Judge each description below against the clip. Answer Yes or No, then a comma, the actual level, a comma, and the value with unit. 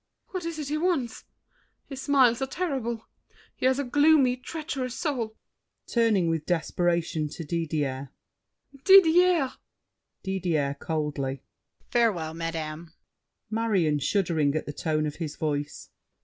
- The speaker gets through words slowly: Yes, slow, 120 wpm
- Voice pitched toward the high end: Yes, high, 195 Hz